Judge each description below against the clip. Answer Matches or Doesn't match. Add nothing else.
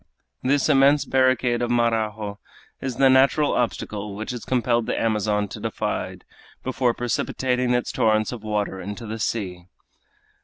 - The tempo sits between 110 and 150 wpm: Matches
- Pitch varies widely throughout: Doesn't match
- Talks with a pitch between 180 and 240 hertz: Doesn't match